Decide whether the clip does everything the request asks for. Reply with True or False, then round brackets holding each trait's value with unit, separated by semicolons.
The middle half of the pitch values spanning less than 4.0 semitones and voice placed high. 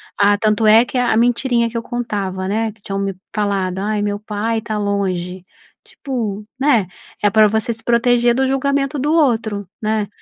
True (2.9 semitones; 220 Hz)